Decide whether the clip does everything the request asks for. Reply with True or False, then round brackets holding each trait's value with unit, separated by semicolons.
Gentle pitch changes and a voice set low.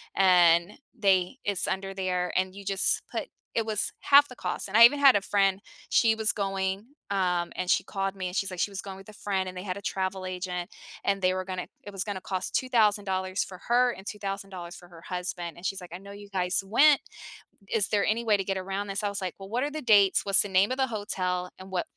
False (1.8 semitones; 195 Hz)